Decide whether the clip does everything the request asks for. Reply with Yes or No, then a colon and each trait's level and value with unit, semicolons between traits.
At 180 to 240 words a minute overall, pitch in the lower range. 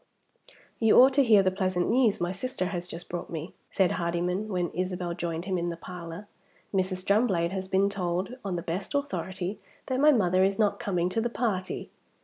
No: average, 195 wpm; medium, 185 Hz